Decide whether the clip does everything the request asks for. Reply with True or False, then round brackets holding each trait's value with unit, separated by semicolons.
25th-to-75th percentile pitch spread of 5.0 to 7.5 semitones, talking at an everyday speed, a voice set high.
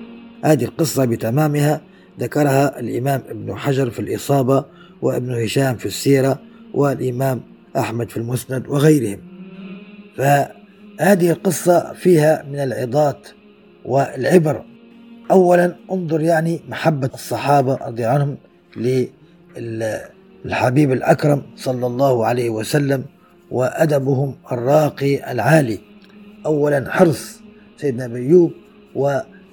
False (5.5 semitones; 90 wpm; 145 Hz)